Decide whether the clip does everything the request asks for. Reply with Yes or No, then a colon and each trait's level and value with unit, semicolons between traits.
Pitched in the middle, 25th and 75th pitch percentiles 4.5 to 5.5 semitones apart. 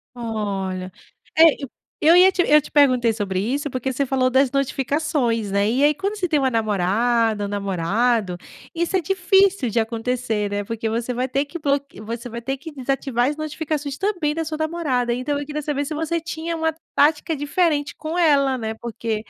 No: very high, 270 Hz; average, 5.2 semitones